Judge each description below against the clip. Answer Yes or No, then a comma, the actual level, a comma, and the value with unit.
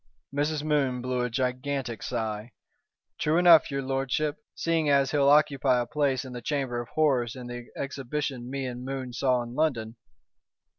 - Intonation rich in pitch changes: No, average, 2.9 semitones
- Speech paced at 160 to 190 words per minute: Yes, average, 165 wpm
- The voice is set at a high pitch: No, low, 135 Hz